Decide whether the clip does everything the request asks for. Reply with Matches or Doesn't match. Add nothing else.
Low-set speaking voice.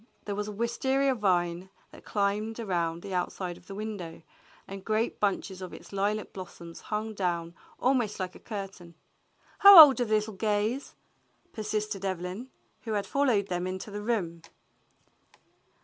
Doesn't match